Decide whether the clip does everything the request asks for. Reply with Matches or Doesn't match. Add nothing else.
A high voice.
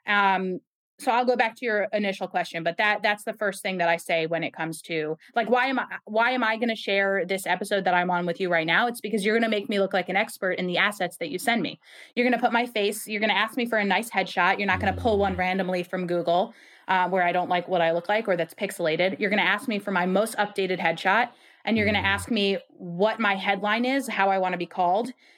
Matches